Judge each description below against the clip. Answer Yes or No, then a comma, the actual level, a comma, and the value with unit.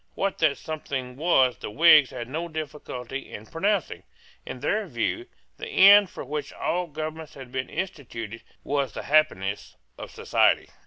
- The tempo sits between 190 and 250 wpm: No, average, 155 wpm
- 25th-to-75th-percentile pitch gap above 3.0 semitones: Yes, average, 4.9 semitones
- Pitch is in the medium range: Yes, medium, 150 Hz